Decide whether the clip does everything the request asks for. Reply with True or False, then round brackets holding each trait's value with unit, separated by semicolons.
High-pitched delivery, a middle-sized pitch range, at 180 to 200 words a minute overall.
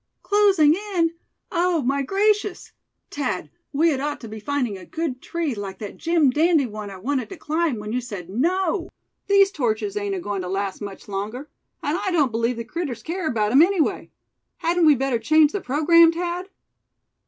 False (290 Hz; 7.0 semitones; 185 wpm)